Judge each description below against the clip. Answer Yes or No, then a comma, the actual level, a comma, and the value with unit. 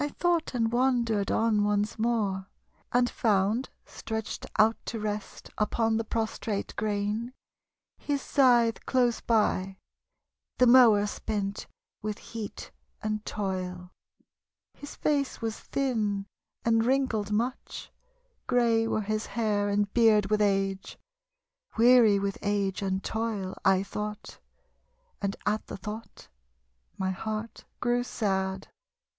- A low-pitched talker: No, high, 215 Hz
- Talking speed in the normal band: No, slow, 120 wpm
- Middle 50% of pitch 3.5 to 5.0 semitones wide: No, narrow, 2.5 semitones